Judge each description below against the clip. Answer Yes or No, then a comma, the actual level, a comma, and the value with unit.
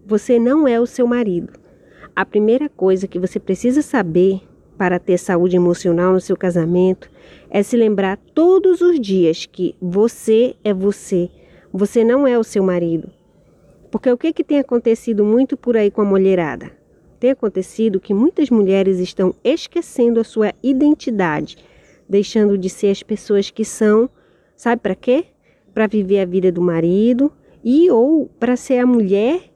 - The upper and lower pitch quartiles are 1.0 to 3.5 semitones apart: No, average, 4.5 semitones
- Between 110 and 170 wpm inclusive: Yes, average, 165 wpm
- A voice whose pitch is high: Yes, high, 210 Hz